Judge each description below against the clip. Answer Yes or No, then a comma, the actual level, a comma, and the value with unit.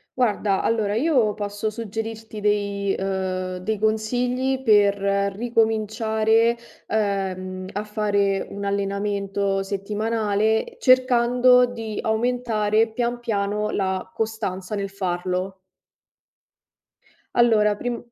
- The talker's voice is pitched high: Yes, high, 210 Hz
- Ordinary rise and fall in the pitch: No, narrow, 2.2 semitones